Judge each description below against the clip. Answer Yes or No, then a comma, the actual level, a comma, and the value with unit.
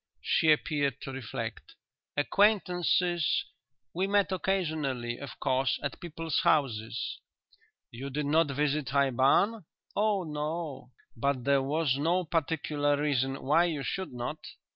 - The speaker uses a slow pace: Yes, slow, 125 wpm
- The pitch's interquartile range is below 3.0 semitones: No, average, 3.8 semitones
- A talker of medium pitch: Yes, medium, 150 Hz